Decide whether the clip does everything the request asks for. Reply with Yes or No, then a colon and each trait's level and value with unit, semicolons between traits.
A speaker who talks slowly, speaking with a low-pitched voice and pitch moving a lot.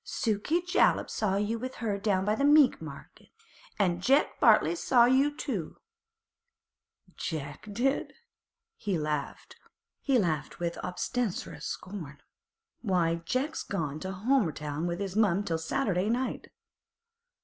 No: slow, 120 wpm; high, 200 Hz; wide, 6.6 semitones